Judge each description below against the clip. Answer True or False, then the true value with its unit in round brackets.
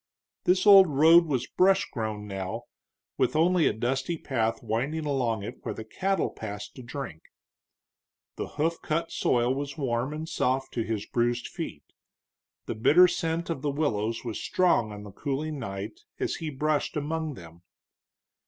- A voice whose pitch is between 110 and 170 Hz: True (135 Hz)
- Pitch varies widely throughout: True (6.0 semitones)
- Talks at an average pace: True (160 wpm)